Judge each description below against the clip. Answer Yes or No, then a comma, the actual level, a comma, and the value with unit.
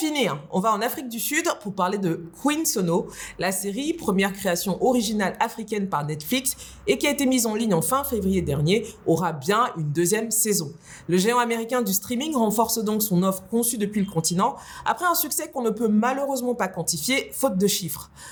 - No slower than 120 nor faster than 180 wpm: No, average, 205 wpm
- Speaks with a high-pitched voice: Yes, high, 215 Hz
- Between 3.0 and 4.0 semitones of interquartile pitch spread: No, average, 5.3 semitones